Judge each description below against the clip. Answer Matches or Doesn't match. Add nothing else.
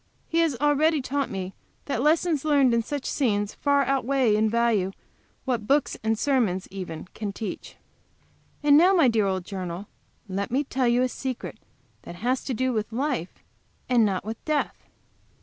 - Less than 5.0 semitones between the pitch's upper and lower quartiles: Doesn't match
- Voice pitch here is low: Doesn't match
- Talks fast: Doesn't match